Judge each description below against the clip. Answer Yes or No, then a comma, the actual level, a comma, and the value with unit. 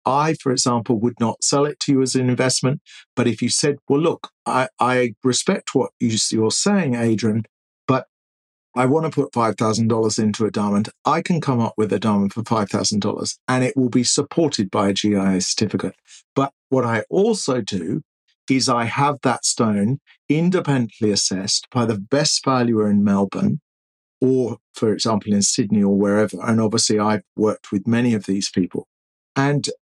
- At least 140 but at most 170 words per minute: No, average, 185 wpm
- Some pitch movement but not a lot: Yes, average, 4.0 semitones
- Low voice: Yes, low, 115 Hz